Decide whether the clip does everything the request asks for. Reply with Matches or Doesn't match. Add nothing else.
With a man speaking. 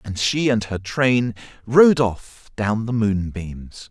Matches